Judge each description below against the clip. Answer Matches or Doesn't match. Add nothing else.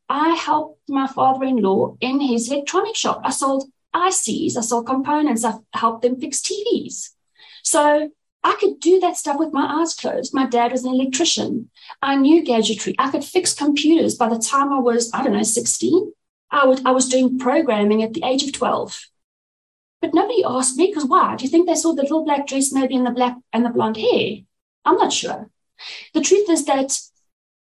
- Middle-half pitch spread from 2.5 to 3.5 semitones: Doesn't match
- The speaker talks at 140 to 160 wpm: Doesn't match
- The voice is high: Matches